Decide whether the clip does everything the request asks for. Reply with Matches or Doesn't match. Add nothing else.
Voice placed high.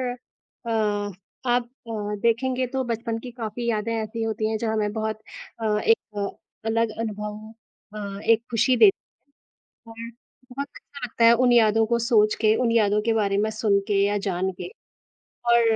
Matches